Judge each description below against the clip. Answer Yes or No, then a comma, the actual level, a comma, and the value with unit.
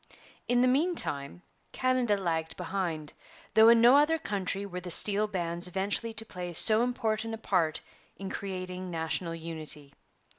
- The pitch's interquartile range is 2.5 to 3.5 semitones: No, average, 5.0 semitones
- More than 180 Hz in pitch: Yes, high, 190 Hz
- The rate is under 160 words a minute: Yes, average, 150 wpm